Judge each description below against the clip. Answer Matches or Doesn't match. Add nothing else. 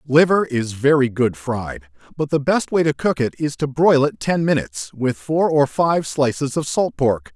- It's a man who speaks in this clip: Matches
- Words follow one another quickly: Matches